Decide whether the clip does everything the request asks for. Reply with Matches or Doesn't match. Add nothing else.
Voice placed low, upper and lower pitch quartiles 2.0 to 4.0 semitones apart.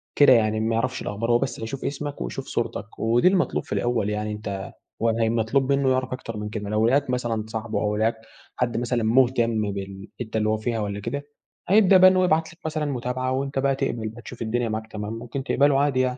Matches